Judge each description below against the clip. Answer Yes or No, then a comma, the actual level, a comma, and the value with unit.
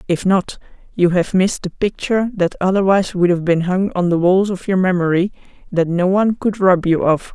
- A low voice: No, medium, 185 Hz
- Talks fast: Yes, fast, 210 wpm